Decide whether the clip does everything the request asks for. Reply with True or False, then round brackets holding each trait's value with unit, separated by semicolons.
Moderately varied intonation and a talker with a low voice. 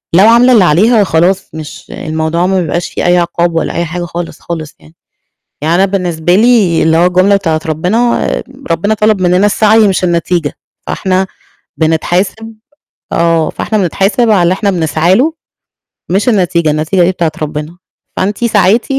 False (3.5 semitones; 180 Hz)